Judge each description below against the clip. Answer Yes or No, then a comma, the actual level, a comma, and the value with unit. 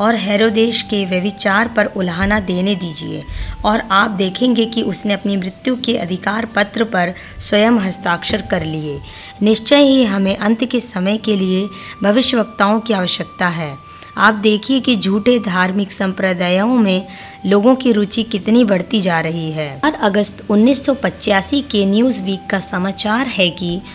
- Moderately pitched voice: No, high, 200 Hz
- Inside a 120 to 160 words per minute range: Yes, average, 150 wpm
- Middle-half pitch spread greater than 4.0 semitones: No, average, 3.1 semitones